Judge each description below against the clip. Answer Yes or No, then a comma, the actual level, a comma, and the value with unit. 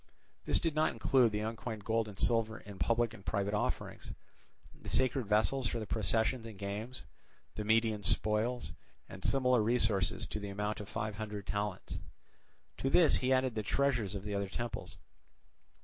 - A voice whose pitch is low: Yes, low, 110 Hz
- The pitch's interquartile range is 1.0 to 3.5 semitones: Yes, narrow, 2.6 semitones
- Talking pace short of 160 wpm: No, average, 170 wpm